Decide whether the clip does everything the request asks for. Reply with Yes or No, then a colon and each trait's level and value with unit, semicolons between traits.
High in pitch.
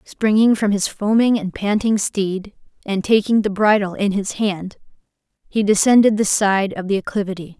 Yes: high, 205 Hz